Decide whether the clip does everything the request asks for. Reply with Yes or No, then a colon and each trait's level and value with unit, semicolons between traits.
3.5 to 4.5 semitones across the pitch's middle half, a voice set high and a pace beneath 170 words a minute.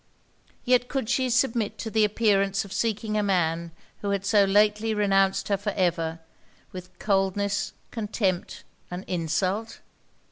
No: narrow, 2.4 semitones; high, 200 Hz; average, 140 wpm